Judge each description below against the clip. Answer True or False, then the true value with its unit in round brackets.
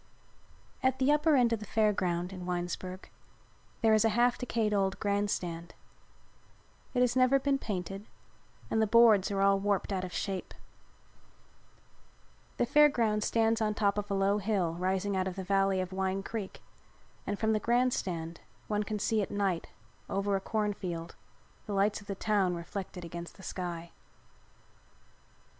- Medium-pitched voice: False (200 Hz)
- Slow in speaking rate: False (170 wpm)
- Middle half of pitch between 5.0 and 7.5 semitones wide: False (2.9 semitones)